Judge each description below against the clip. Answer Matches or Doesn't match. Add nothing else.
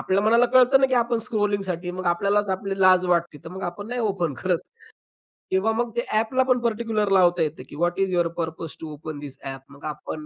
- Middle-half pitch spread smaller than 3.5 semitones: Doesn't match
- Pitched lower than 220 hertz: Matches